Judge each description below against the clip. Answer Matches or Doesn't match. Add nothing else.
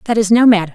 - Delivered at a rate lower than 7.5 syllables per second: Doesn't match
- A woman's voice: Matches